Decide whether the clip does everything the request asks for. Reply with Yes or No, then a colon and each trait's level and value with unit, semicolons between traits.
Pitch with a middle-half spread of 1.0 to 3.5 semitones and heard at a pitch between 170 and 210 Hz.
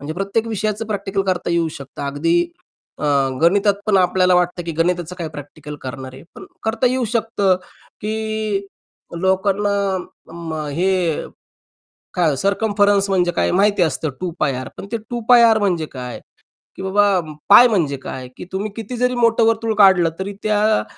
No: average, 4.3 semitones; high, 190 Hz